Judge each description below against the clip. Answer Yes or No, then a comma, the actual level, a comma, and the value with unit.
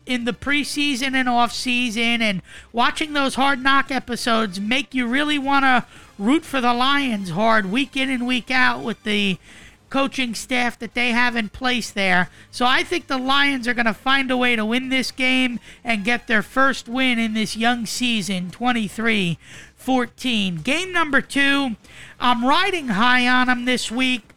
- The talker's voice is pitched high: Yes, very high, 250 Hz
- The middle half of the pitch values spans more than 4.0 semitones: No, average, 2.8 semitones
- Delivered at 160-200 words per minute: Yes, average, 175 wpm